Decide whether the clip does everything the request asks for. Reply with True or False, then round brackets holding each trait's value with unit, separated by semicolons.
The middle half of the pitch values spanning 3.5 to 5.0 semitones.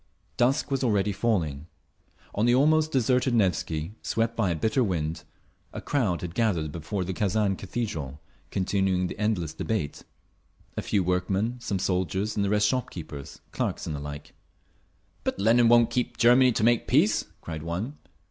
False (5.4 semitones)